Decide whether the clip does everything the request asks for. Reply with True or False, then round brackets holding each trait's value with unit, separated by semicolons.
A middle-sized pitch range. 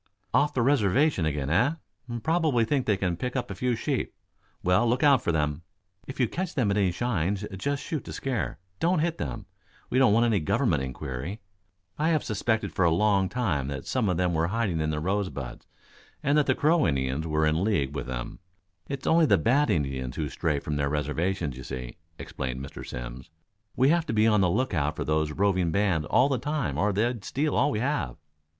False (8.6 semitones)